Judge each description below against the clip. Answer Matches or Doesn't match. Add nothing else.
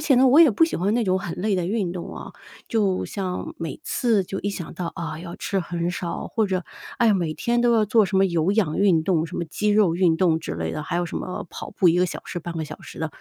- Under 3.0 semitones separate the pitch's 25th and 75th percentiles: Doesn't match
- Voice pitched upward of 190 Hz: Doesn't match